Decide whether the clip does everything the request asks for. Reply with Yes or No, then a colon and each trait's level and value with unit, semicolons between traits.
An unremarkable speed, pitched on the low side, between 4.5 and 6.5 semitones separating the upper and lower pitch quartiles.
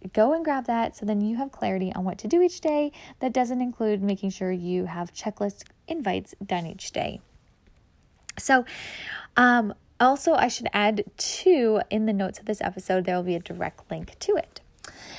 No: average, 190 wpm; high, 215 Hz; average, 5.3 semitones